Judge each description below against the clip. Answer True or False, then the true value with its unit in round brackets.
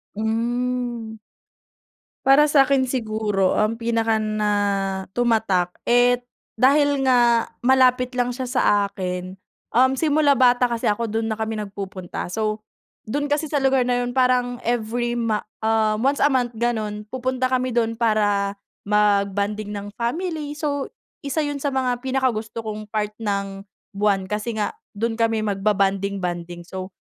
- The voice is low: False (230 Hz)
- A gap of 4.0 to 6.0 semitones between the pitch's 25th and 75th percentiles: False (3.4 semitones)